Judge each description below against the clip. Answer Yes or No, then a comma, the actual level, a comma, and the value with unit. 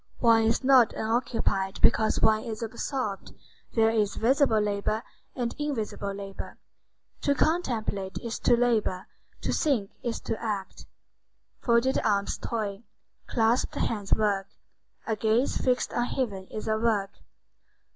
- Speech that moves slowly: Yes, slow, 130 wpm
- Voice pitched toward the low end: No, high, 225 Hz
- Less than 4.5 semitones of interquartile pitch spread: Yes, average, 2.9 semitones